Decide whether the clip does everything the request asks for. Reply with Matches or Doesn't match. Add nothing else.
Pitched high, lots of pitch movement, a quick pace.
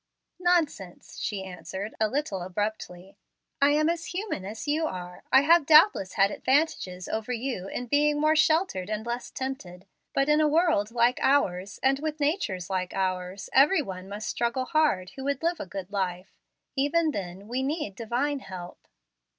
Doesn't match